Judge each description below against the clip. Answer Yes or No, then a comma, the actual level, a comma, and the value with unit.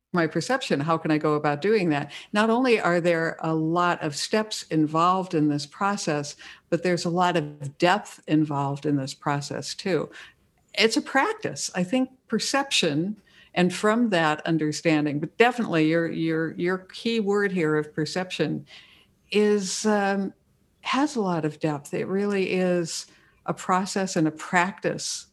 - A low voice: No, medium, 175 Hz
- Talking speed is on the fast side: No, average, 160 wpm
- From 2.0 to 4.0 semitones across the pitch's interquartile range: No, average, 4.7 semitones